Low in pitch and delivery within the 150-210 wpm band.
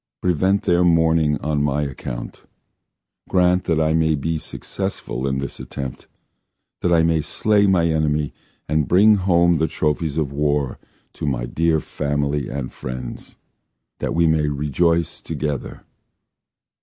No: very low, 80 Hz; average, 140 wpm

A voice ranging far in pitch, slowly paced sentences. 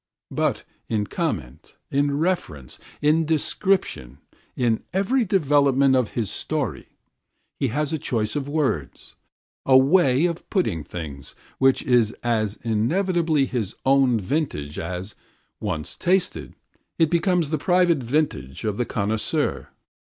Yes: wide, 7.0 semitones; slow, 125 wpm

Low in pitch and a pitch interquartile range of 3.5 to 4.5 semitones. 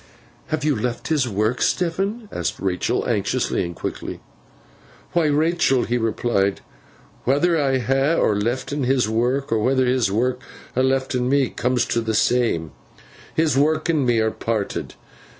Yes: low, 130 Hz; average, 4.1 semitones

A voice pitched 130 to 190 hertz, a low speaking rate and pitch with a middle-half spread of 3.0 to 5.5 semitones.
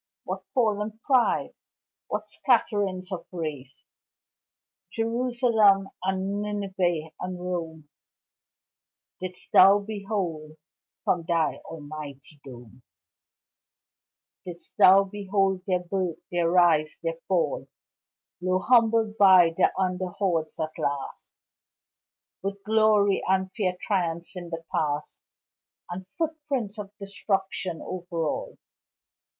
Yes: medium, 185 Hz; slow, 100 wpm; average, 3.5 semitones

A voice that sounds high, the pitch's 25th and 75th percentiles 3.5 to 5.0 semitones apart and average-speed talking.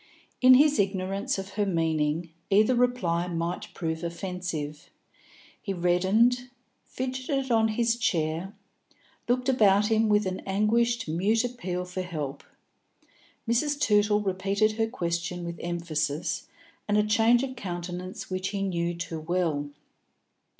No: high, 195 Hz; average, 4.6 semitones; slow, 130 wpm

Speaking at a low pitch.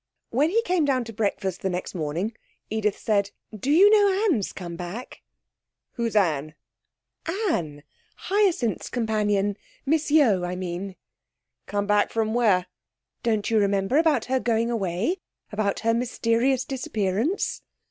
No: high, 220 Hz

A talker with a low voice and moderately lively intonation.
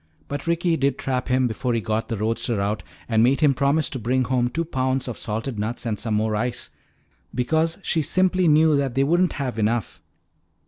Yes: low, 130 Hz; average, 4.6 semitones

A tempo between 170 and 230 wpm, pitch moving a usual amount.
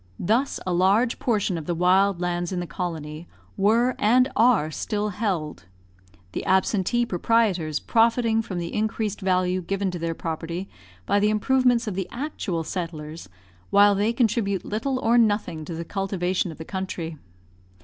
No: average, 160 wpm; average, 4.3 semitones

